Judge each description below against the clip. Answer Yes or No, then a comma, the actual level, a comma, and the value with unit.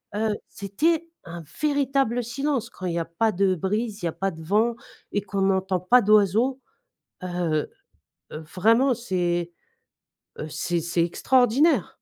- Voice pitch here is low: No, high, 205 Hz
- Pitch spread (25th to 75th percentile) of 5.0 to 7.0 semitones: Yes, wide, 5.6 semitones